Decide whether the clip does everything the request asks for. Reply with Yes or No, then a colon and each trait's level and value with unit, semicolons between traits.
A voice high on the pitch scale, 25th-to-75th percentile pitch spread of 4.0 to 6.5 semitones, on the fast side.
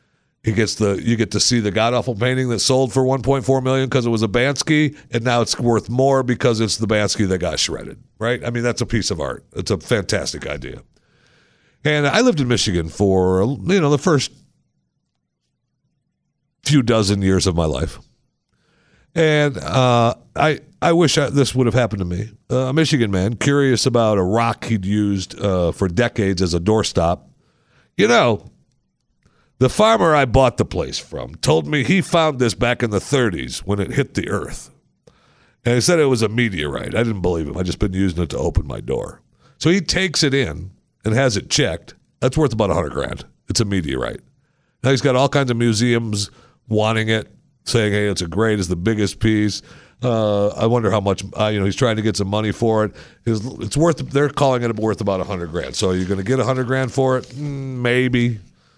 No: low, 115 Hz; average, 4.4 semitones; fast, 210 wpm